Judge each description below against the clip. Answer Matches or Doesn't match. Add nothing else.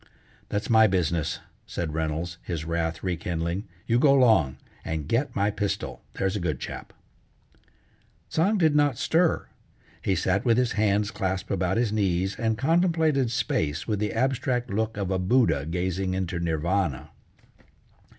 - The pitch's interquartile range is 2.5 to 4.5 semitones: Doesn't match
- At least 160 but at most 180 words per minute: Doesn't match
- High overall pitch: Doesn't match